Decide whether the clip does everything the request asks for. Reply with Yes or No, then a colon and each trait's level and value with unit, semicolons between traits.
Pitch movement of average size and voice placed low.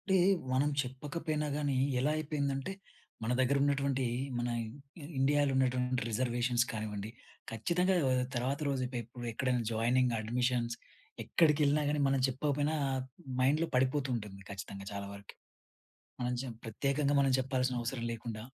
Yes: average, 3.1 semitones; low, 130 Hz